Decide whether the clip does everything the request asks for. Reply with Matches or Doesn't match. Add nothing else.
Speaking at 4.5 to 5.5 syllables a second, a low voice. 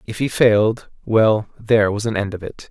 Matches